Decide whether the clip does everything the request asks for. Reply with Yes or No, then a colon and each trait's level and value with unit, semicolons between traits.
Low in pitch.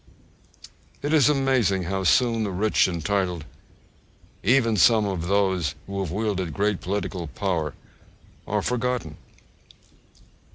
Yes: low, 100 Hz